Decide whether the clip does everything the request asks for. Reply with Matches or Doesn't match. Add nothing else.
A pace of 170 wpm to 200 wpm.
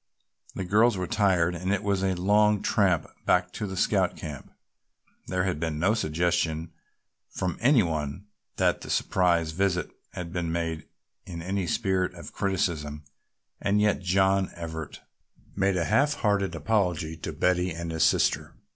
Doesn't match